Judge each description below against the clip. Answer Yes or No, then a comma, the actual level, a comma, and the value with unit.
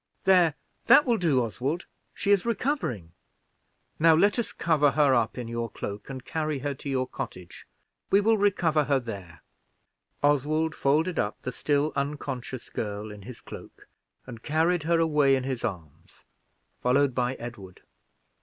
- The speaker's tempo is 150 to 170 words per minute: Yes, average, 155 wpm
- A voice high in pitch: No, medium, 140 Hz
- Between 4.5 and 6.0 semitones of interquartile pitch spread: Yes, average, 5.1 semitones